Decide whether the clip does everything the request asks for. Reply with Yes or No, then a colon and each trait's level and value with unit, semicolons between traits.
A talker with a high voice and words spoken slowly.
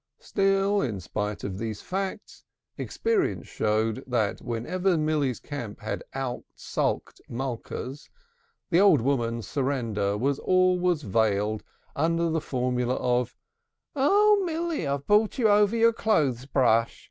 No: medium, 140 Hz; slow, 125 wpm